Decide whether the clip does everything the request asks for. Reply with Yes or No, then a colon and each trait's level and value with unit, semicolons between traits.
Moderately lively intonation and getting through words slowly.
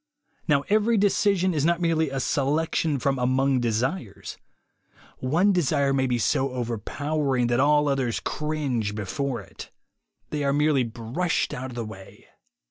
No: average, 3.9 semitones; average, 150 wpm